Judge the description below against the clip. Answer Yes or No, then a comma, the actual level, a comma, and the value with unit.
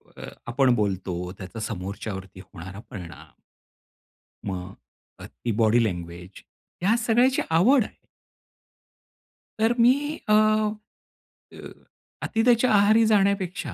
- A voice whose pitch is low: Yes, low, 115 Hz